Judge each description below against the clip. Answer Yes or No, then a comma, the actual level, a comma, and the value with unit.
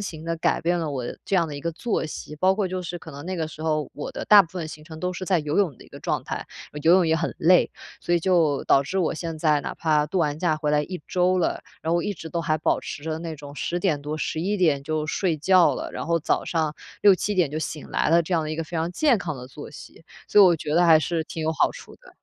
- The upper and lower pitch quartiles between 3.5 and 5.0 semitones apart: No, average, 2.7 semitones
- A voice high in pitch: No, medium, 165 Hz